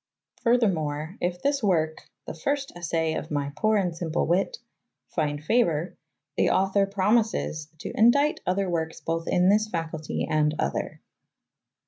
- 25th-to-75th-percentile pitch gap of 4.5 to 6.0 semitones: Yes, average, 5.2 semitones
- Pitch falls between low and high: Yes, medium, 175 Hz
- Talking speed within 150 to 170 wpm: No, average, 140 wpm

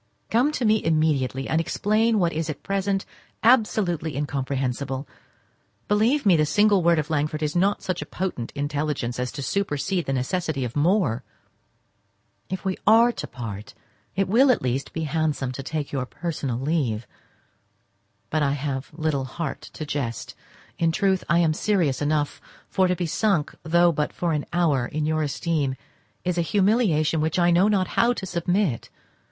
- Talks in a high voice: No, medium, 160 Hz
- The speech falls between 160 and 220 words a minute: Yes, average, 170 wpm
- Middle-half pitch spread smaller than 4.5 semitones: No, average, 5.0 semitones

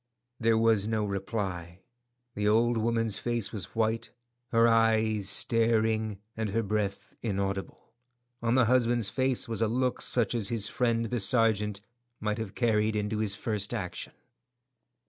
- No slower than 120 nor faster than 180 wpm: Yes, average, 145 wpm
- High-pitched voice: No, low, 110 Hz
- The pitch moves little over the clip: Yes, narrow, 1.8 semitones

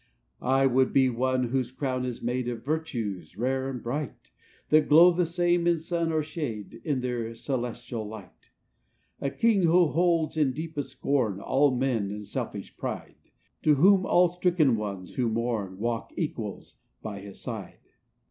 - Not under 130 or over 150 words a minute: No, average, 165 wpm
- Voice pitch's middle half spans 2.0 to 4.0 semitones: No, average, 5.3 semitones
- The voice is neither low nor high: No, low, 130 Hz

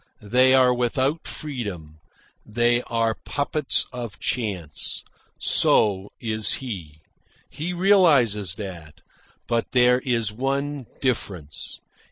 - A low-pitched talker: Yes, low, 120 Hz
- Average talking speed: No, slow, 100 wpm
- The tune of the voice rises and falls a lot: No, average, 4.5 semitones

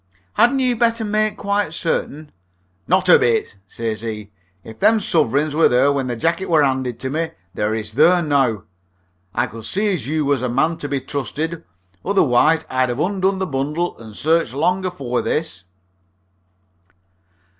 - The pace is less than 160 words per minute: No, average, 170 wpm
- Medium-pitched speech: Yes, medium, 145 Hz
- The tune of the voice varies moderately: No, wide, 6.5 semitones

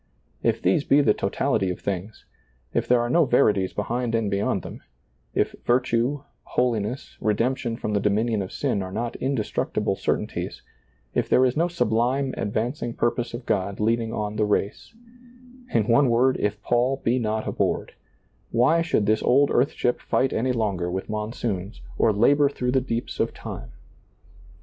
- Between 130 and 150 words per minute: No, average, 175 wpm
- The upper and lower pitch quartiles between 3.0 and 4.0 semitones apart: Yes, average, 3.5 semitones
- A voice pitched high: No, low, 115 Hz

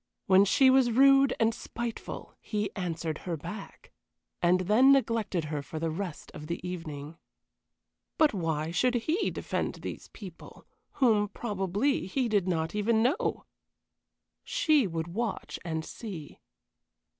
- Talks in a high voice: Yes, high, 200 Hz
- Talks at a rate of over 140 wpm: No, slow, 135 wpm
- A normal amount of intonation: No, wide, 6.2 semitones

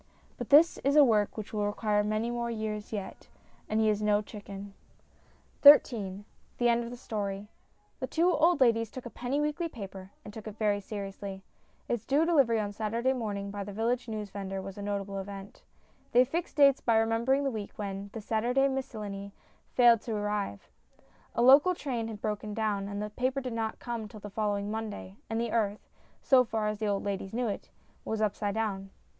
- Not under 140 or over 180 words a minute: No, average, 195 wpm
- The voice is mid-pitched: No, high, 215 Hz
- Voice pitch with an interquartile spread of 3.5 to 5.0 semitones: No, average, 2.9 semitones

